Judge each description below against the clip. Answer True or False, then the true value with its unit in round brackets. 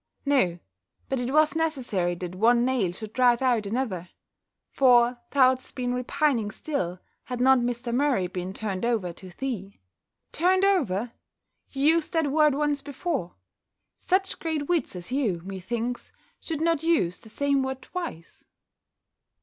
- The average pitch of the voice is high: True (250 Hz)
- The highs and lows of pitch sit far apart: True (6.0 semitones)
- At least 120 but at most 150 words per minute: True (145 wpm)